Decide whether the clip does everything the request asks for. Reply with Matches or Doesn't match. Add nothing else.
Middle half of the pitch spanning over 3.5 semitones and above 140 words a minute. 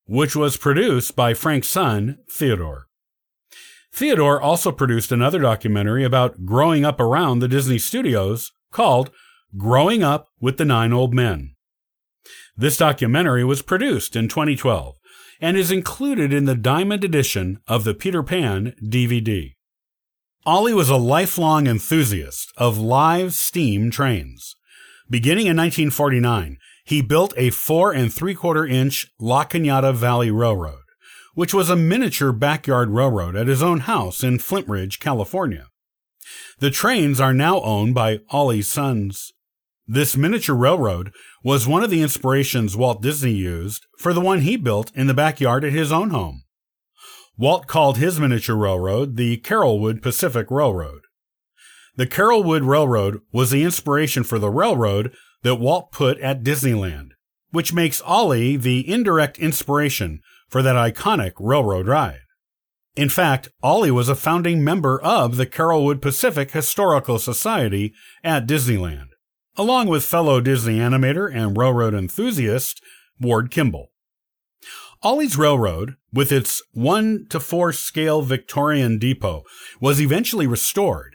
Doesn't match